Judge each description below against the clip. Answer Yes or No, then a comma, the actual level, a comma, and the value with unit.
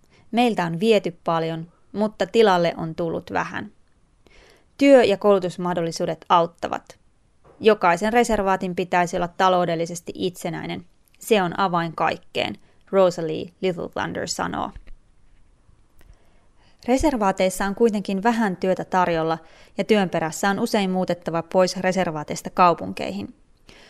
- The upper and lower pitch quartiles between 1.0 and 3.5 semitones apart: Yes, average, 3.2 semitones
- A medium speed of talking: Yes, average, 105 wpm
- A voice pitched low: No, medium, 185 Hz